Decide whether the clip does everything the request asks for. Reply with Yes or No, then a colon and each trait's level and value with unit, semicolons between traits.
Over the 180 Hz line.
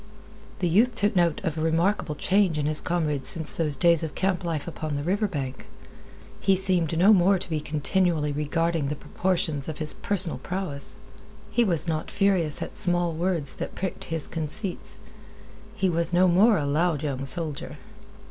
No: medium, 170 Hz